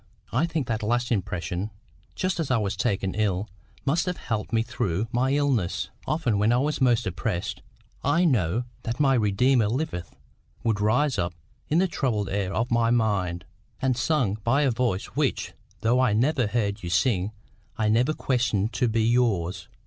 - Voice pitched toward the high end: No, low, 115 Hz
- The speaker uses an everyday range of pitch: Yes, average, 4.3 semitones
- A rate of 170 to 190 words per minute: Yes, average, 175 wpm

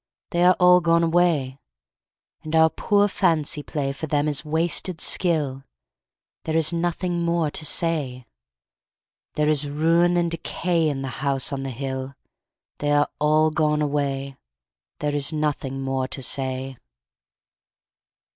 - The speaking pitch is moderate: Yes, medium, 150 Hz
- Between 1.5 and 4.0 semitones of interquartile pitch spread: Yes, average, 3.5 semitones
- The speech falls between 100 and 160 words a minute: Yes, average, 140 wpm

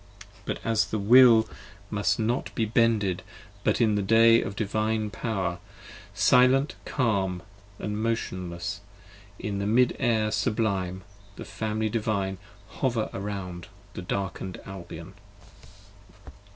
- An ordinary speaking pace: No, slow, 120 wpm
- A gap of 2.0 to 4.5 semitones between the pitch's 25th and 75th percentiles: Yes, average, 2.7 semitones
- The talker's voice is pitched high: No, low, 105 Hz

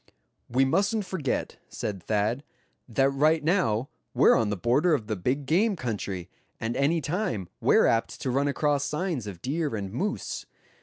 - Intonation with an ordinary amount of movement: No, wide, 6.4 semitones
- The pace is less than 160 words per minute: No, average, 165 wpm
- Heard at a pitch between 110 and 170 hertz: Yes, low, 135 Hz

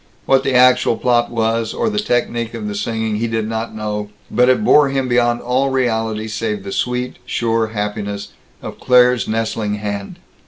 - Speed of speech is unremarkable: Yes, average, 175 wpm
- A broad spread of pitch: No, narrow, 2.5 semitones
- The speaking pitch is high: No, low, 115 Hz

